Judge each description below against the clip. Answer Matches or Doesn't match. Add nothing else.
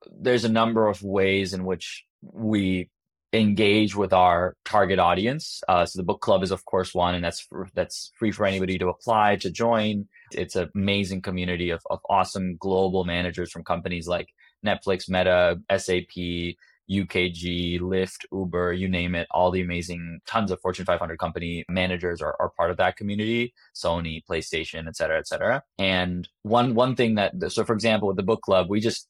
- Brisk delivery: Doesn't match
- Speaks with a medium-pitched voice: Doesn't match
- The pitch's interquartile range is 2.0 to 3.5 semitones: Matches